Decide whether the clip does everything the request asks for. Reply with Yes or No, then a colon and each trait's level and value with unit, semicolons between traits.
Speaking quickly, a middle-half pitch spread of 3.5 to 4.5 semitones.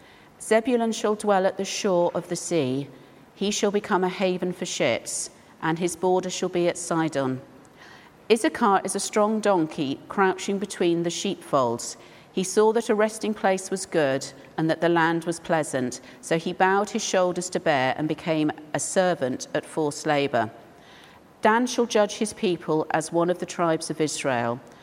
No: average, 175 wpm; average, 4.0 semitones